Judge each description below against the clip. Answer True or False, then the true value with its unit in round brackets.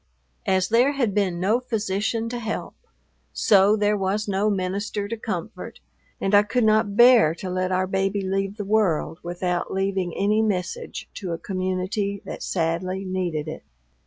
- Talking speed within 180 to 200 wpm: False (160 wpm)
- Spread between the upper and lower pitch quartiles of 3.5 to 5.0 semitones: False (2.5 semitones)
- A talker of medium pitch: False (195 Hz)